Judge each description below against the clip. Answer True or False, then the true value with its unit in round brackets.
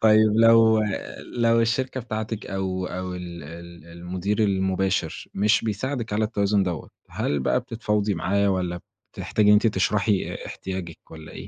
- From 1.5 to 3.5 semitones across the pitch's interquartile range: True (3.2 semitones)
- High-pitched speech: False (100 Hz)